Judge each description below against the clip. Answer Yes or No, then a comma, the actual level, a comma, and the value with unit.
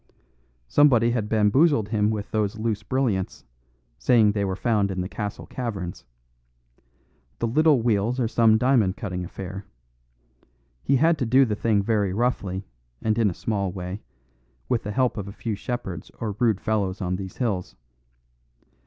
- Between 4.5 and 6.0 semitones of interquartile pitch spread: No, average, 3.3 semitones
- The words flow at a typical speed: Yes, average, 160 wpm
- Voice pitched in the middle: No, low, 110 Hz